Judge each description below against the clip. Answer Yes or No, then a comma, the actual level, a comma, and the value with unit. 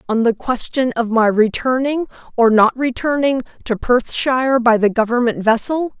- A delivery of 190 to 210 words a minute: No, average, 150 wpm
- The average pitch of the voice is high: Yes, high, 245 Hz